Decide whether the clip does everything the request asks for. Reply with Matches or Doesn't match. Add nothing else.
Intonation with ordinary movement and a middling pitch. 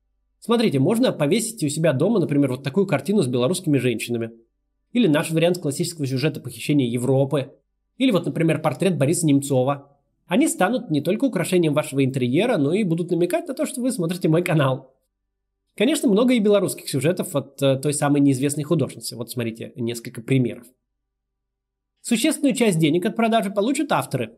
Doesn't match